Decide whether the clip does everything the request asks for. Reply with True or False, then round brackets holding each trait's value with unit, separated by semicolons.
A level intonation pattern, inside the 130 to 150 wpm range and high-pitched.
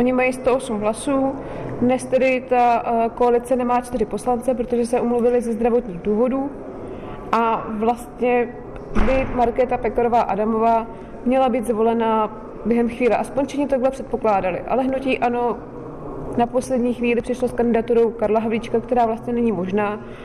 True (1.8 semitones; 140 wpm; 240 Hz)